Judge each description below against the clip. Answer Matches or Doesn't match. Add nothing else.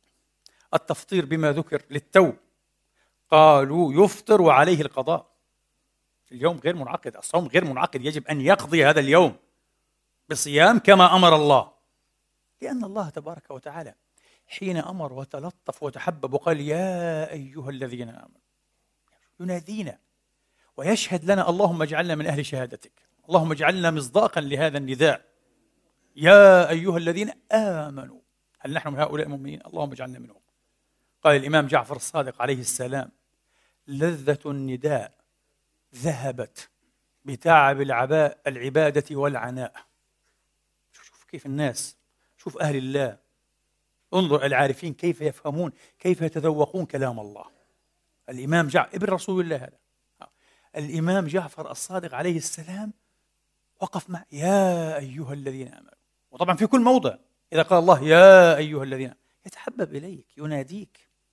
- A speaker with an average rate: Matches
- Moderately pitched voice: Matches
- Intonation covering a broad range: Doesn't match